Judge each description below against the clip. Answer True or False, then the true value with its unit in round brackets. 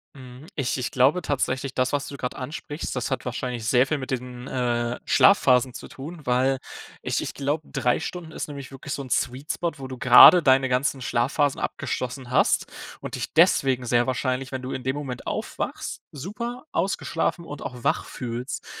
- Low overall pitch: True (130 Hz)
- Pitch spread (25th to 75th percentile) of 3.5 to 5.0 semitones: False (2.4 semitones)